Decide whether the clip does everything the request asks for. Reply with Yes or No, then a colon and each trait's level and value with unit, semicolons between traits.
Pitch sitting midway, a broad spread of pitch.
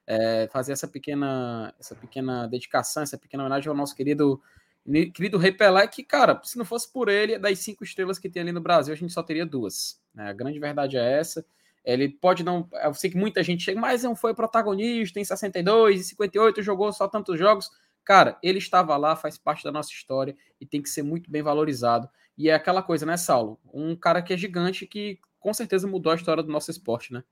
Yes: medium, 170 Hz; wide, 5.7 semitones